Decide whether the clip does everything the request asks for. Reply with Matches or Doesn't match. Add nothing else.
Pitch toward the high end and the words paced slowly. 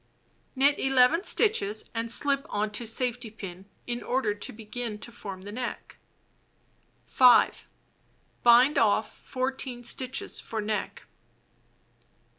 Matches